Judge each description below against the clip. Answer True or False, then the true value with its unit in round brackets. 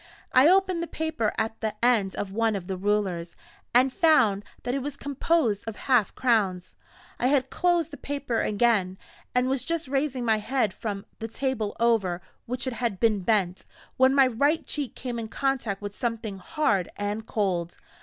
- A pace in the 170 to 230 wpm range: True (180 wpm)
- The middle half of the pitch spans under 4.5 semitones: False (4.8 semitones)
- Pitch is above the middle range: True (230 Hz)